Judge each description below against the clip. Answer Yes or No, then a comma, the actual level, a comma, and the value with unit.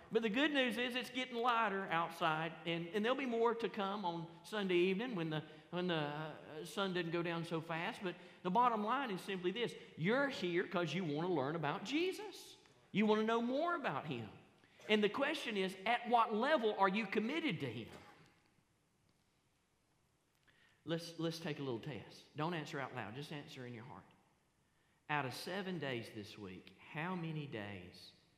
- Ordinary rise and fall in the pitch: No, wide, 6.6 semitones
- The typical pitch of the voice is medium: Yes, medium, 180 Hz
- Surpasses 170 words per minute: Yes, average, 185 wpm